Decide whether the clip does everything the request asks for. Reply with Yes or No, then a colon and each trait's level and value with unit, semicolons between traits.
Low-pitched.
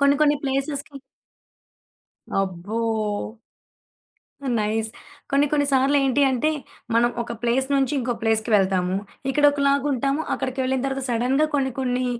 No: very high, 265 Hz